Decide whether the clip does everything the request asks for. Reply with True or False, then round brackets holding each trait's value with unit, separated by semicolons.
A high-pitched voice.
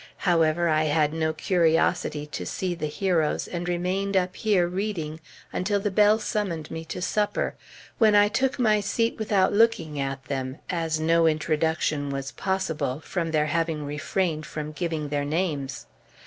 False (165 Hz)